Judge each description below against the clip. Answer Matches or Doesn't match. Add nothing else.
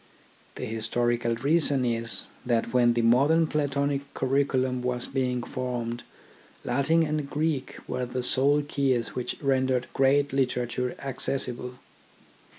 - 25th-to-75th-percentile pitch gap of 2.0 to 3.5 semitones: Matches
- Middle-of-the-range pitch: Doesn't match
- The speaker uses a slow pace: Matches